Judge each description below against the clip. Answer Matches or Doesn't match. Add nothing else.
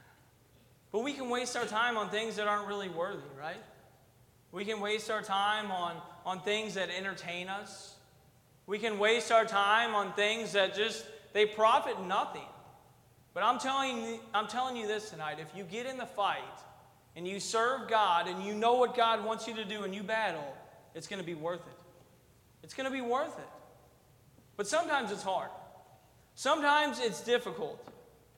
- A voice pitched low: Doesn't match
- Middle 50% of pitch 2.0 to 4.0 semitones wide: Doesn't match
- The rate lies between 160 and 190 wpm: Matches